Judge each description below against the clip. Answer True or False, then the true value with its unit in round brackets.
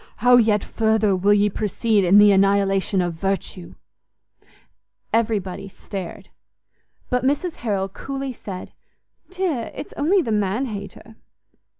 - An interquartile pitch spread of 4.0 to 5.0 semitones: False (3.5 semitones)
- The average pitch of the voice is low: False (210 Hz)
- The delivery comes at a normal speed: False (120 wpm)